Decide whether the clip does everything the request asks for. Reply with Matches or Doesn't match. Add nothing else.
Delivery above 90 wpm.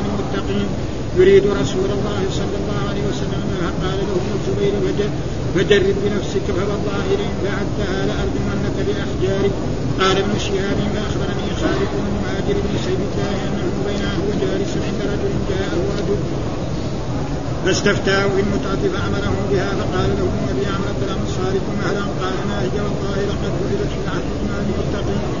Matches